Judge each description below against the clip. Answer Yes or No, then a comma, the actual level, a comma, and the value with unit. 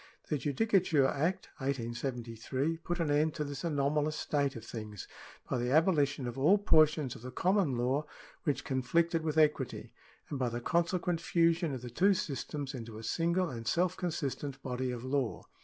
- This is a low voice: No, medium, 145 Hz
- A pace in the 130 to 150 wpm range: No, average, 175 wpm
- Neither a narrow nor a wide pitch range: Yes, average, 4.6 semitones